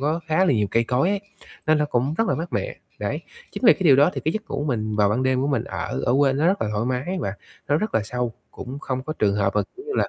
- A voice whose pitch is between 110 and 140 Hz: Yes, low, 135 Hz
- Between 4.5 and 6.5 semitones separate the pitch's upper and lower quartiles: Yes, wide, 5.4 semitones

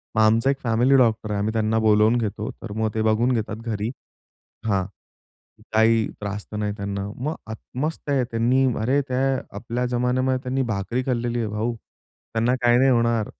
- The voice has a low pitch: Yes, low, 115 Hz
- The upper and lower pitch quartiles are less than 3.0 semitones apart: Yes, narrow, 2.4 semitones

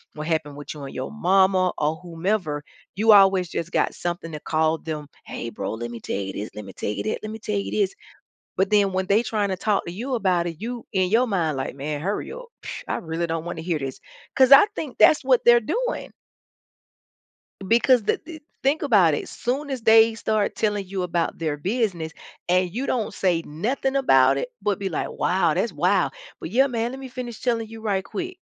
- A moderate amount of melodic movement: No, wide, 6.0 semitones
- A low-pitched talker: No, high, 190 Hz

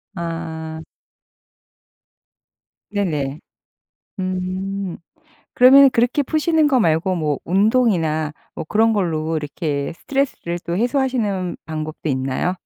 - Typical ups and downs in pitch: No, wide, 6.1 semitones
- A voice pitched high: No, medium, 180 Hz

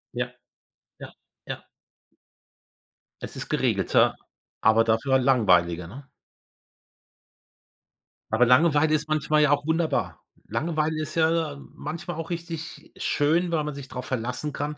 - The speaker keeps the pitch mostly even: No, average, 3.9 semitones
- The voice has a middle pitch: Yes, medium, 150 Hz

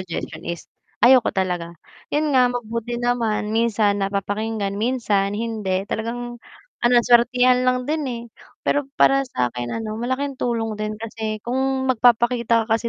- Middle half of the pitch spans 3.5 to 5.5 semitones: No, narrow, 2.6 semitones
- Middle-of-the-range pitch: No, high, 230 Hz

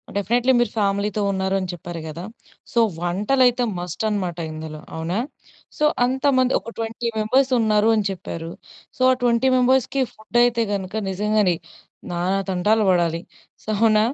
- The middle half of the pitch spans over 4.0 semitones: Yes, average, 4.9 semitones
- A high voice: Yes, high, 210 Hz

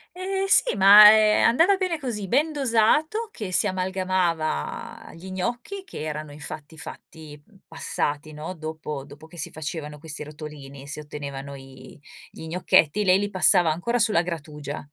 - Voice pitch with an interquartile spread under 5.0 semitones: No, wide, 6.0 semitones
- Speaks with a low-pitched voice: No, medium, 170 Hz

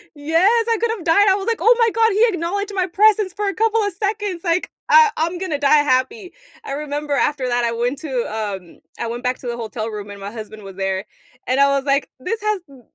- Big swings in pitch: Yes, wide, 8.8 semitones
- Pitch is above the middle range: Yes, very high, 315 Hz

